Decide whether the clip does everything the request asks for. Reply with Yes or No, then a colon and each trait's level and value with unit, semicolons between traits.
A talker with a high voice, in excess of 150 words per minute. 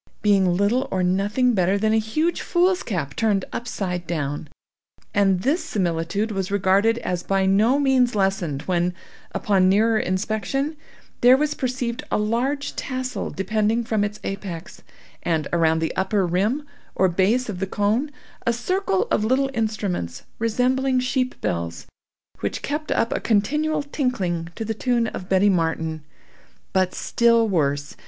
No: high, 210 Hz; average, 145 wpm